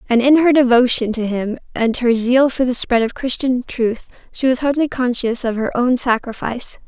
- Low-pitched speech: No, high, 245 Hz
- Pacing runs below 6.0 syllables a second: Yes, 5.0 syllables/s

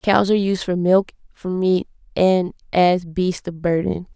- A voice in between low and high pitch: Yes, medium, 180 Hz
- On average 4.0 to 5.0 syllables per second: Yes, 4.1 syllables/s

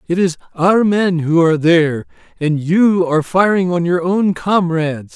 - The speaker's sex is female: No, male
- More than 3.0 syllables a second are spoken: Yes, 4.6 syllables/s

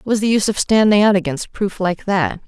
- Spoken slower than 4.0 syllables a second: No, 6.0 syllables/s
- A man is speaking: No, female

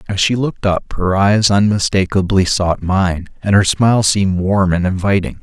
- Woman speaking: No, male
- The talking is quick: No, average, 175 wpm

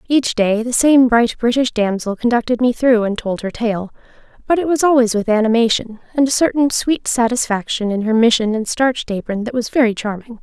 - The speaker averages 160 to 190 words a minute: No, average, 200 wpm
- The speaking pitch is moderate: No, high, 235 Hz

